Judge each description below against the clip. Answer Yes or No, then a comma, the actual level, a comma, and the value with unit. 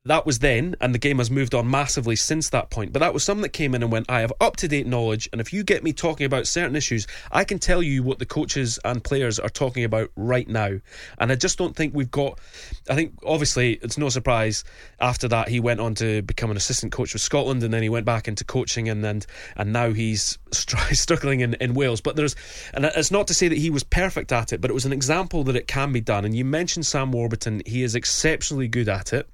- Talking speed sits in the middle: No, fast, 260 wpm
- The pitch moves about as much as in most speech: Yes, average, 4.3 semitones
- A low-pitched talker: Yes, low, 125 Hz